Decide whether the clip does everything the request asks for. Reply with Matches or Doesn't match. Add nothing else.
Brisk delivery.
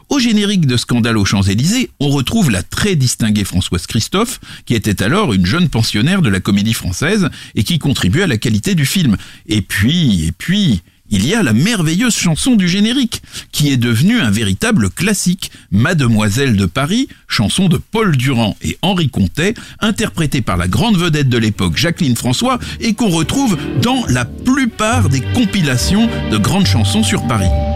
Doesn't match